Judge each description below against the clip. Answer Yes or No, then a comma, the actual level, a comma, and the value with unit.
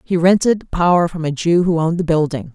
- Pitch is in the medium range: Yes, medium, 165 Hz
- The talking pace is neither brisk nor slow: No, fast, 235 wpm